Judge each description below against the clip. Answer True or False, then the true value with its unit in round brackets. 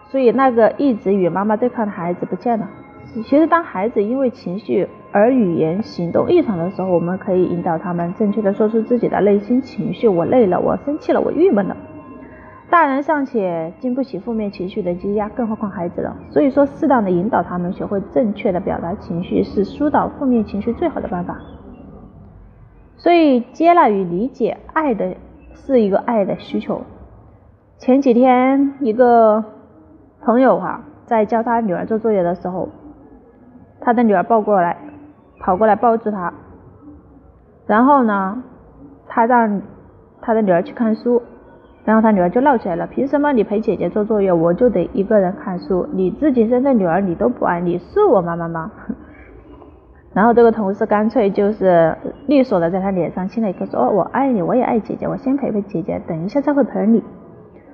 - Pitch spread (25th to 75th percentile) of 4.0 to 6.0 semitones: True (5.1 semitones)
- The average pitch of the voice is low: False (220 Hz)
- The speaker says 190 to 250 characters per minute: False (280 characters per minute)